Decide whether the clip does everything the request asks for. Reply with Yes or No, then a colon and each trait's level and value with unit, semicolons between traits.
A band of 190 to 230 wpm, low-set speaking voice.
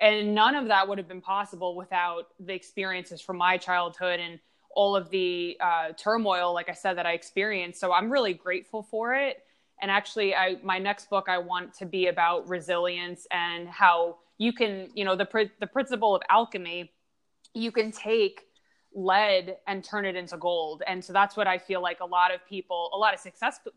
No: average, 200 wpm; high, 190 Hz